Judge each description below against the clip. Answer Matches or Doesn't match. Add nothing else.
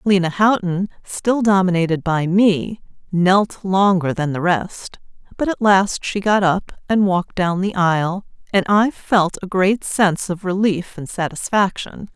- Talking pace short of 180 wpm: Matches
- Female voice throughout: Matches